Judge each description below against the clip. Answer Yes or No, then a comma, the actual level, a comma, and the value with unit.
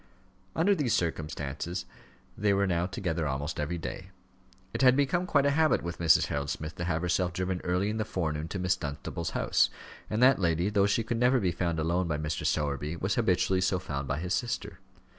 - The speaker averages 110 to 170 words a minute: No, fast, 205 wpm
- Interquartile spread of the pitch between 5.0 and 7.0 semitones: No, average, 4.6 semitones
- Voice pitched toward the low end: Yes, very low, 90 Hz